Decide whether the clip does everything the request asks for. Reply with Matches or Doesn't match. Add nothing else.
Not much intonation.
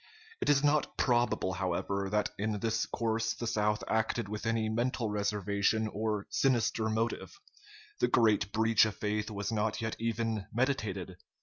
Matches